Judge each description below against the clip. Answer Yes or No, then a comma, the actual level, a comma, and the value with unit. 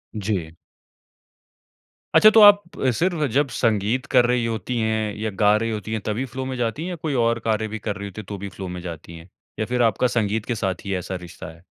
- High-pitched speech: No, low, 110 Hz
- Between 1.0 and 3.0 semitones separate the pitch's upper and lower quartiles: No, average, 3.7 semitones